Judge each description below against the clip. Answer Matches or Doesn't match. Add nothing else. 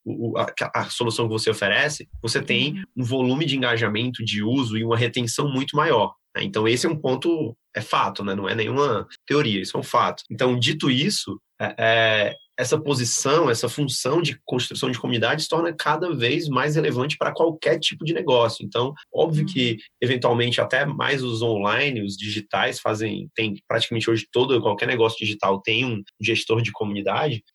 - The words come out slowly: Doesn't match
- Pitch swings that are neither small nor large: Matches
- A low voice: Matches